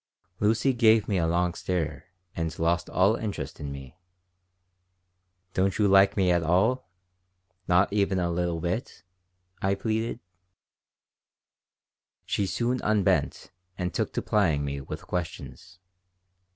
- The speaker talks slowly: Yes, slow, 125 wpm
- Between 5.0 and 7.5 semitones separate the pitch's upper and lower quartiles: No, average, 3.5 semitones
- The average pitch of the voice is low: Yes, very low, 95 Hz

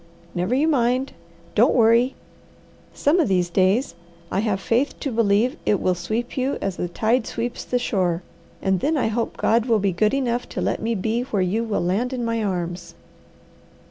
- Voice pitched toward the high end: Yes, high, 225 Hz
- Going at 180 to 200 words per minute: Yes, average, 190 wpm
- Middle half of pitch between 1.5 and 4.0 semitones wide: No, average, 4.4 semitones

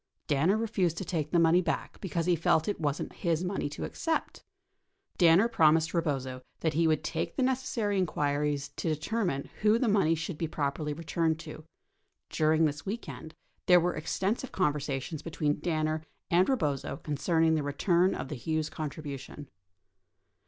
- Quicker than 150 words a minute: Yes, average, 160 wpm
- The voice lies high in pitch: No, medium, 160 Hz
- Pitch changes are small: No, average, 3.3 semitones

